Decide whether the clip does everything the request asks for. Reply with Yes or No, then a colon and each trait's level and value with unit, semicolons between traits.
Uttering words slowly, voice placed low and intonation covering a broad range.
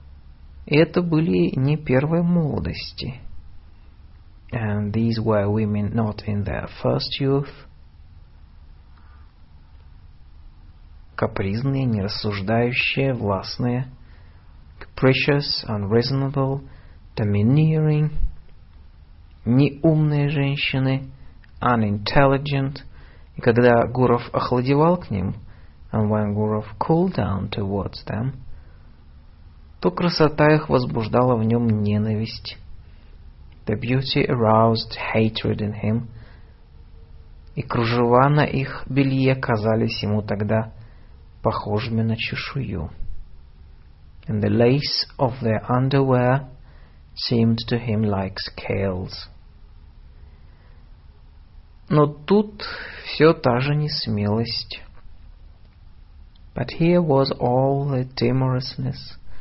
Yes: slow, 85 wpm; low, 110 Hz; wide, 7.5 semitones